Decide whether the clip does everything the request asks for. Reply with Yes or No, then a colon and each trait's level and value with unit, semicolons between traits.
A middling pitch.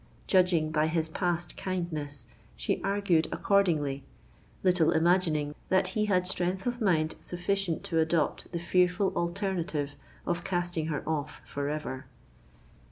Yes: medium, 175 Hz